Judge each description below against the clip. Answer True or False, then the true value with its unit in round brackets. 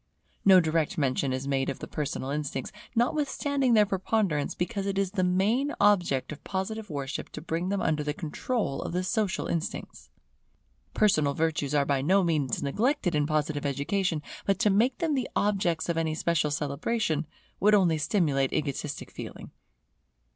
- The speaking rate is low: False (165 wpm)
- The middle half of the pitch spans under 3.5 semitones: False (5.6 semitones)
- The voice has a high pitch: False (170 Hz)